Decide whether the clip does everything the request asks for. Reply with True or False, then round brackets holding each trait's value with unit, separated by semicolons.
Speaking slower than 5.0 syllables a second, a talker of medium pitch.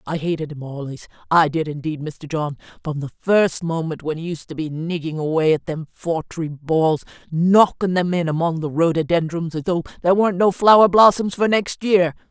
False (5.1 syllables/s; 165 Hz)